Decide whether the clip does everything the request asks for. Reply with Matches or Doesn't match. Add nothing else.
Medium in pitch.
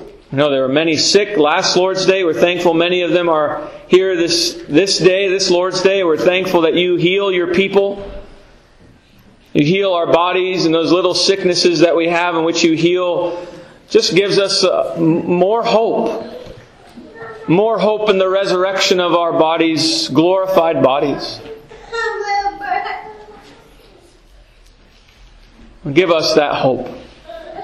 Matches